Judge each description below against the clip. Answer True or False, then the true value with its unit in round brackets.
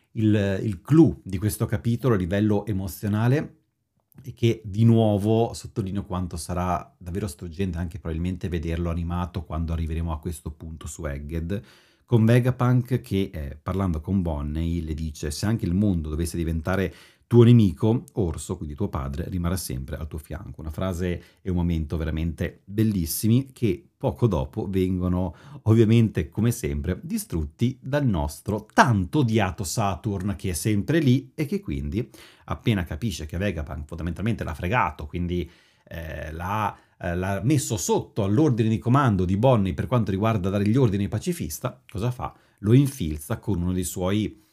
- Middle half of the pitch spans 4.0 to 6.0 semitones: True (4.9 semitones)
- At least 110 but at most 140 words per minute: False (155 wpm)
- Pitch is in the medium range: False (95 Hz)